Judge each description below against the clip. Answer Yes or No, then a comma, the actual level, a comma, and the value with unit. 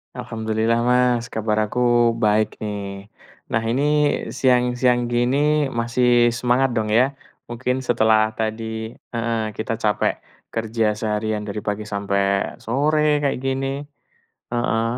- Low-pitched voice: Yes, low, 115 Hz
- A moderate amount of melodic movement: No, narrow, 2.3 semitones